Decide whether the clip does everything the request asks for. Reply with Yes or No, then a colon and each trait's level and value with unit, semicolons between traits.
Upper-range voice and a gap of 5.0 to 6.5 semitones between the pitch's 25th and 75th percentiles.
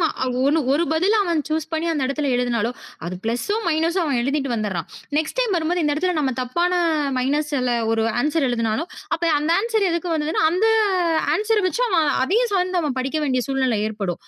Yes: very high, 305 Hz; wide, 5.6 semitones